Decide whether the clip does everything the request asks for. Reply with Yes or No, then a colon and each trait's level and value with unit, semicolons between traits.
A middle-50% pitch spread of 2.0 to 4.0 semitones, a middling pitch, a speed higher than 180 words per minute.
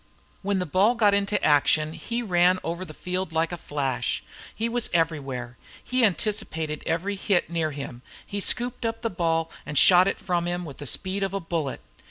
No: average, 4.4 semitones; medium, 175 Hz; average, 200 wpm